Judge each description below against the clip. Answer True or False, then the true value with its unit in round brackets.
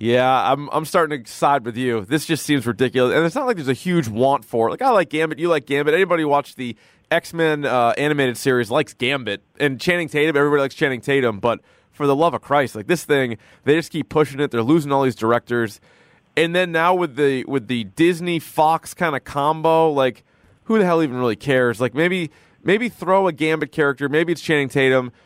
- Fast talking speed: True (225 wpm)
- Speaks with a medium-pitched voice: True (145 Hz)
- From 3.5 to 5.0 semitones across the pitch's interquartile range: True (4.1 semitones)